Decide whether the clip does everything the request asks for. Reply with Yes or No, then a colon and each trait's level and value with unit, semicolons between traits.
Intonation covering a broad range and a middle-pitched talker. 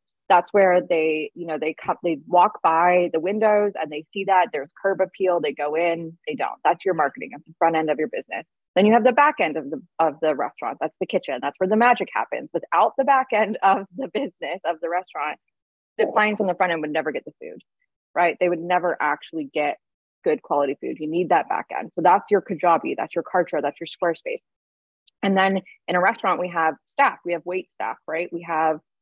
No: average, 3.4 semitones; medium, 175 Hz